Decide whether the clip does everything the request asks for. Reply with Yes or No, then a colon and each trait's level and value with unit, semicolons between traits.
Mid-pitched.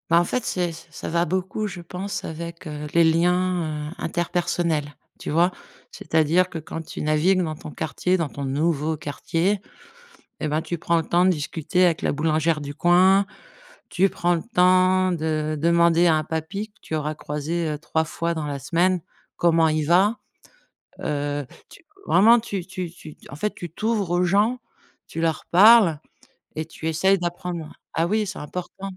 Yes: medium, 170 Hz